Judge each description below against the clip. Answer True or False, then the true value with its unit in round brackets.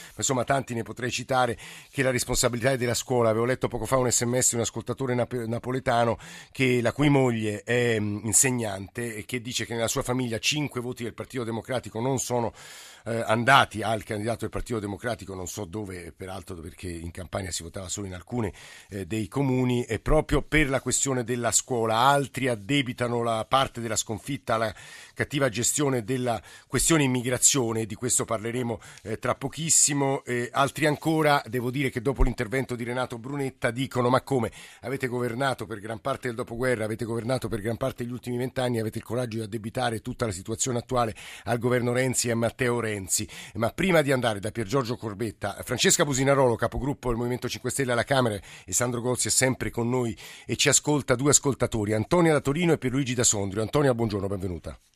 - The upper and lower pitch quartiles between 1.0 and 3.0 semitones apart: True (2.5 semitones)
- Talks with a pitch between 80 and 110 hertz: False (120 Hz)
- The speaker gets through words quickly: True (190 wpm)